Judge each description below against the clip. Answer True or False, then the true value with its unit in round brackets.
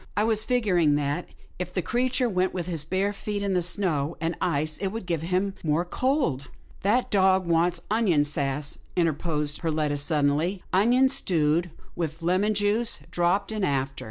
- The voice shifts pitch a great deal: False (4.7 semitones)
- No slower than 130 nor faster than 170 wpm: False (180 wpm)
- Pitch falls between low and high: True (175 Hz)